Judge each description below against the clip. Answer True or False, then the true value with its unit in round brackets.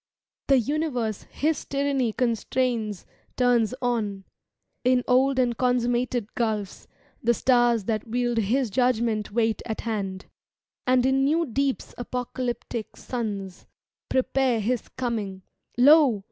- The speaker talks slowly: True (115 wpm)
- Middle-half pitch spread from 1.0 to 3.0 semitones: True (2.7 semitones)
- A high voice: True (240 Hz)